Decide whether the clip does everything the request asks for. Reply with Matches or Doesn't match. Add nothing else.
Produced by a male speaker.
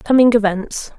Doesn't match